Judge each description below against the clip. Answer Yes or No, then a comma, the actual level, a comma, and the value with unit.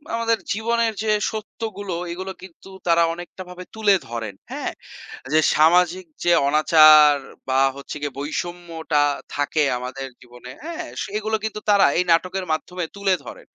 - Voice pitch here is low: No, medium, 175 Hz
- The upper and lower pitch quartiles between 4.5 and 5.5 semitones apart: Yes, average, 5.1 semitones